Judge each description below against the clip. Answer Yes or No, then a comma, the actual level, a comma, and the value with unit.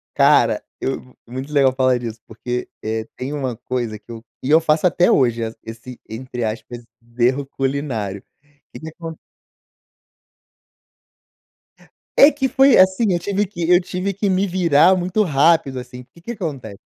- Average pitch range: No, wide, 6.4 semitones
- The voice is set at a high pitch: No, medium, 140 Hz